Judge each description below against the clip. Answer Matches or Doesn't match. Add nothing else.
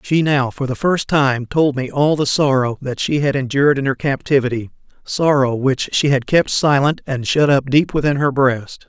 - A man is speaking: Matches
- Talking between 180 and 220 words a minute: Matches